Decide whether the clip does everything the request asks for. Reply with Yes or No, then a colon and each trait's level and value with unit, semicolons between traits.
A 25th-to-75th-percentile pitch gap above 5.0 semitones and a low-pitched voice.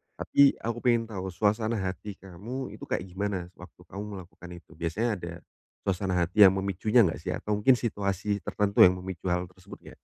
No: average, 2.9 semitones; very low, 95 Hz